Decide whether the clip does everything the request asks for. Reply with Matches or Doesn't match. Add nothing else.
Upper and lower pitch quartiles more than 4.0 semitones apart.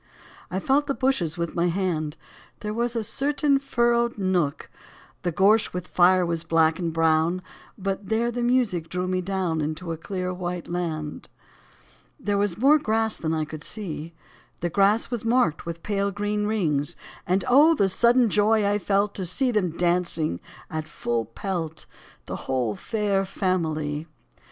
Matches